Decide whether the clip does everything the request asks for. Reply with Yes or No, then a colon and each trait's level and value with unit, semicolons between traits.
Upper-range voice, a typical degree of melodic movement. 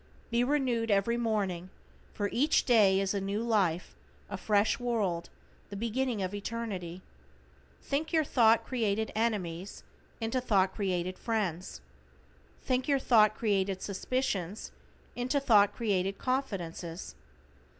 Yes: high, 210 Hz; average, 3.9 semitones